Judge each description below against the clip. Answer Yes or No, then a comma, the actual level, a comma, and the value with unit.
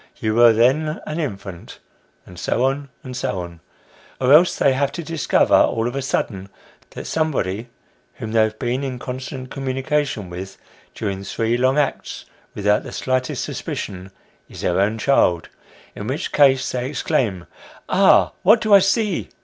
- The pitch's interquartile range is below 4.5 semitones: No, wide, 5.4 semitones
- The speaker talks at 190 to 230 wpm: No, average, 155 wpm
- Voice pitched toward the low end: Yes, low, 125 Hz